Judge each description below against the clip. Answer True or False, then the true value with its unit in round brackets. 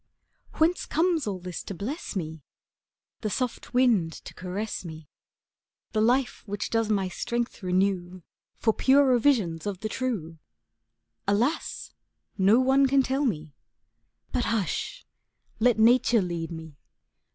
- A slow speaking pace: True (130 wpm)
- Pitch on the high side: True (215 Hz)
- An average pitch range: False (5.8 semitones)